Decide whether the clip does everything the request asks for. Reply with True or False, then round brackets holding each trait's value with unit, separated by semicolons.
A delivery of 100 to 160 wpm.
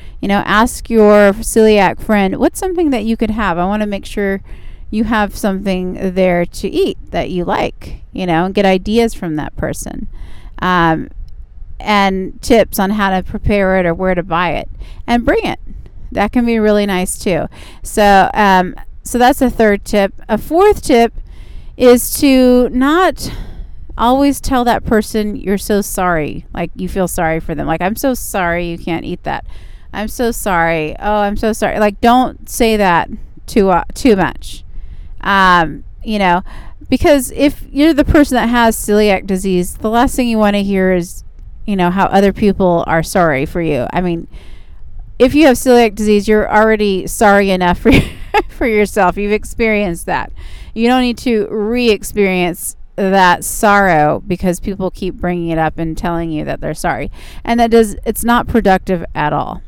False (180 wpm)